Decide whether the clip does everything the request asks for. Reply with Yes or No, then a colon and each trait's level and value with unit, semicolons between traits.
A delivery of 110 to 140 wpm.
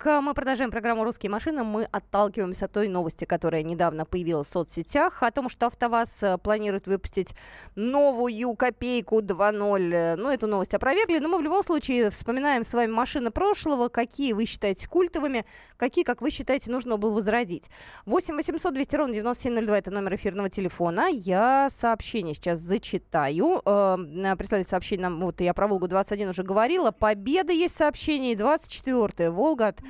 No: average, 155 wpm